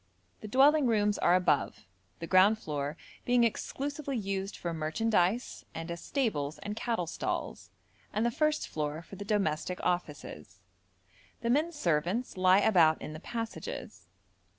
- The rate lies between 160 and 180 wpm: No, average, 145 wpm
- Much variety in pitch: Yes, wide, 6.4 semitones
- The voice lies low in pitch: No, high, 195 Hz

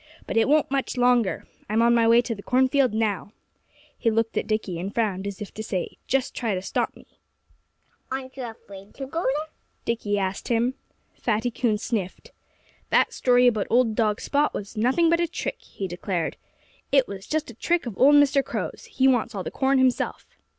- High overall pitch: Yes, high, 235 Hz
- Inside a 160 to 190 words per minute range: No, average, 200 wpm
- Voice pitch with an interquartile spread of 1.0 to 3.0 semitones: No, average, 4.1 semitones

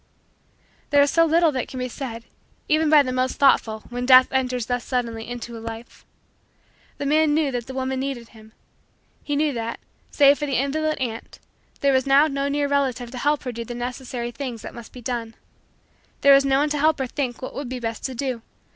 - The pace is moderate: No, fast, 220 wpm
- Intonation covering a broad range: No, average, 2.8 semitones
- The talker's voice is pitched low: No, very high, 260 Hz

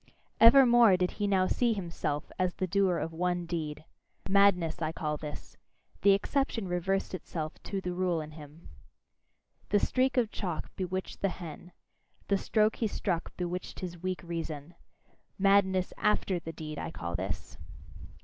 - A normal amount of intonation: Yes, average, 3.4 semitones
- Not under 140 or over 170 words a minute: Yes, average, 155 wpm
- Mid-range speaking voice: Yes, medium, 180 Hz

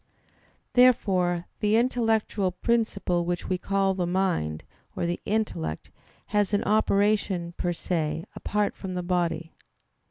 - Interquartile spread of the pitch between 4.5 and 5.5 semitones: No, average, 3.2 semitones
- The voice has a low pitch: No, medium, 185 Hz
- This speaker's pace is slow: Yes, slow, 125 wpm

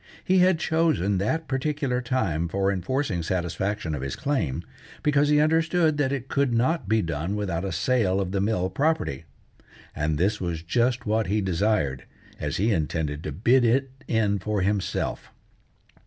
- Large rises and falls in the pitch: Yes, wide, 7.2 semitones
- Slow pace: No, average, 165 wpm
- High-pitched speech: No, low, 105 Hz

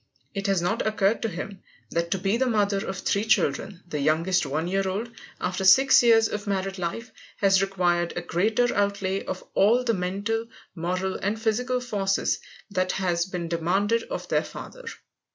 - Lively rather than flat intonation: No, average, 3.3 semitones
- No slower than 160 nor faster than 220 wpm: Yes, average, 175 wpm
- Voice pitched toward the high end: Yes, high, 195 Hz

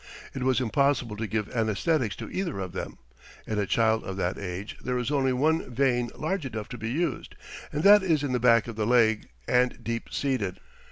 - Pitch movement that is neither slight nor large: Yes, average, 4.0 semitones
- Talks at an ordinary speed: No, fast, 210 wpm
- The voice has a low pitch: Yes, low, 125 Hz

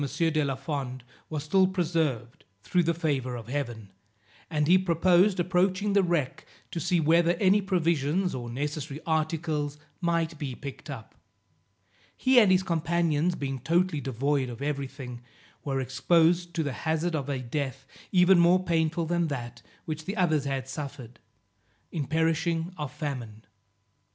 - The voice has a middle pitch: Yes, medium, 155 Hz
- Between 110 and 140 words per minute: No, average, 150 wpm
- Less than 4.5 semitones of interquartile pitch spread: Yes, average, 4.0 semitones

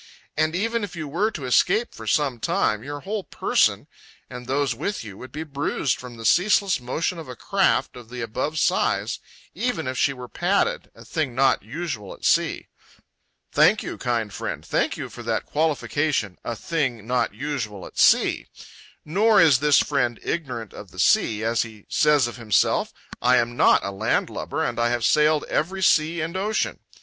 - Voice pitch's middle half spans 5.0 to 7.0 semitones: Yes, wide, 5.4 semitones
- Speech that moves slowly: No, average, 185 wpm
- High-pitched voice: No, medium, 140 Hz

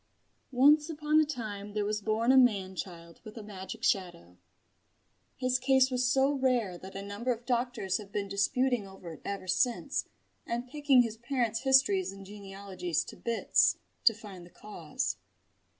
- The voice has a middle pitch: No, high, 220 Hz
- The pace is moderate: Yes, average, 165 wpm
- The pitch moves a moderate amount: Yes, average, 4.5 semitones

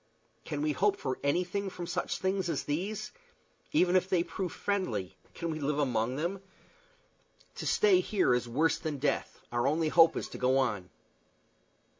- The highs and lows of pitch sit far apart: Yes, wide, 5.8 semitones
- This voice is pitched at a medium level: Yes, medium, 160 Hz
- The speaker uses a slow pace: No, average, 170 wpm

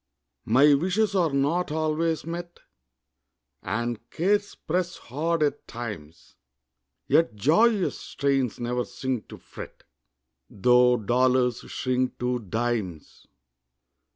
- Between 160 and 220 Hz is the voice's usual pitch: No, low, 135 Hz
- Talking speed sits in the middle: No, slow, 100 wpm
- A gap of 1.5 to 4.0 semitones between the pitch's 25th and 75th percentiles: No, wide, 5.6 semitones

